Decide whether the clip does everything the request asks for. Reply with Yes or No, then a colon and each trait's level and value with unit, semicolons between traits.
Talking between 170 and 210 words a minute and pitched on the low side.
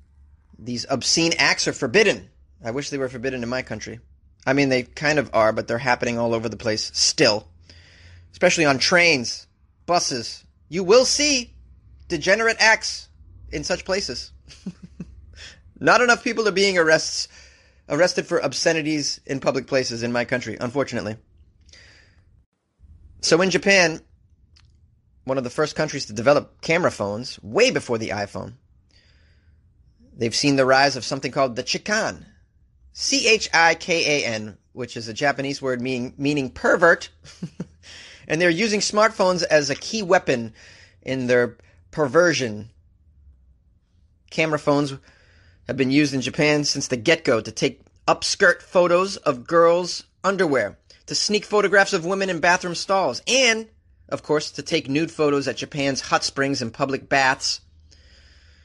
No: average, 145 wpm; low, 130 Hz